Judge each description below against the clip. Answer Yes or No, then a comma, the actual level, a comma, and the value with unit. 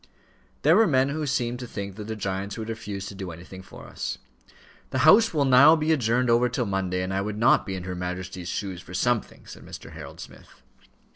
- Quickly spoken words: Yes, fast, 220 wpm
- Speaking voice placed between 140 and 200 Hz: No, low, 110 Hz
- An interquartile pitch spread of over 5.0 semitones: Yes, wide, 5.4 semitones